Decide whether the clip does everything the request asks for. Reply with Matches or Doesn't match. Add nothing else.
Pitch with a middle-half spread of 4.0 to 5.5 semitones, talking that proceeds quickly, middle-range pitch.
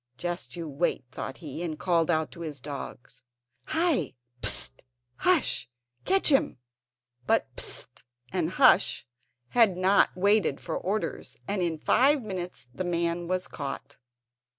Doesn't match